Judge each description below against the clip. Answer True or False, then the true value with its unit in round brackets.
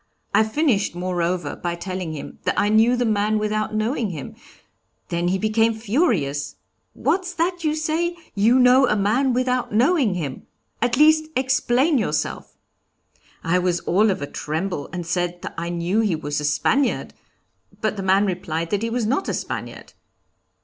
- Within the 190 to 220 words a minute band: False (170 wpm)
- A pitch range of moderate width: False (6.2 semitones)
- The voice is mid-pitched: False (215 Hz)